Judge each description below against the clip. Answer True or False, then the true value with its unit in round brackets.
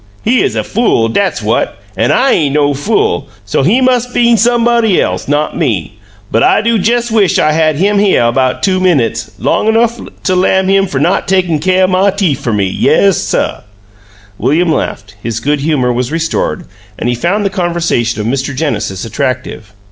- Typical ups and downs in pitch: False (8.0 semitones)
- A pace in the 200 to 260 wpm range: False (190 wpm)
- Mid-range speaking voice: True (165 Hz)